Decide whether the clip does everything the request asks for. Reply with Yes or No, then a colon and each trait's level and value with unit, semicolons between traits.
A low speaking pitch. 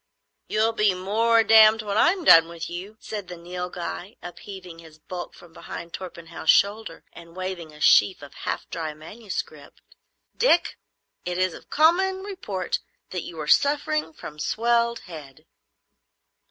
No: medium, 185 Hz